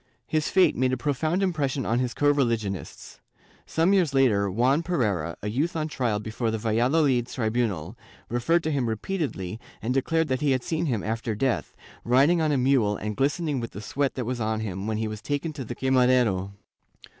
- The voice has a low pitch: Yes, low, 125 Hz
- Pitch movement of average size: Yes, average, 4.9 semitones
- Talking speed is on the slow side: No, average, 195 wpm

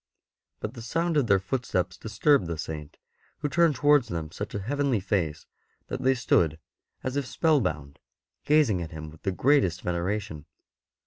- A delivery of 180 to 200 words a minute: No, average, 165 wpm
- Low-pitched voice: Yes, low, 105 Hz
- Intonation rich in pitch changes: Yes, wide, 8.4 semitones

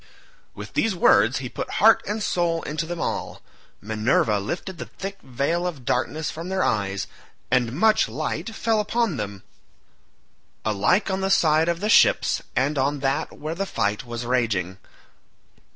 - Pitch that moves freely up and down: Yes, wide, 8.1 semitones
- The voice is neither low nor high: Yes, medium, 155 Hz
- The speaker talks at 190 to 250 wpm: No, average, 160 wpm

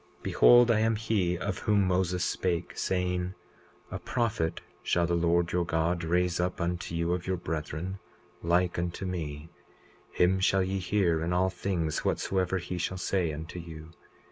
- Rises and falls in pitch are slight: Yes, narrow, 1.9 semitones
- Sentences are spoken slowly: No, average, 170 wpm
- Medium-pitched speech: No, very low, 90 Hz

